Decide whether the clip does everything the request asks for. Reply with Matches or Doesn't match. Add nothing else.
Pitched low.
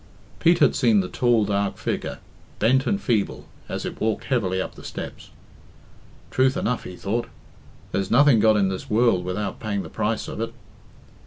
Matches